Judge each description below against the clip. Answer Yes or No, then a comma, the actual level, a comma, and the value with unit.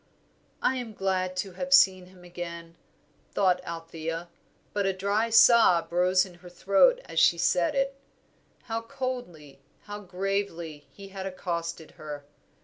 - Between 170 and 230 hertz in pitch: Yes, medium, 185 Hz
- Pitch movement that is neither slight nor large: Yes, average, 3.3 semitones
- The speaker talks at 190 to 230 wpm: No, average, 140 wpm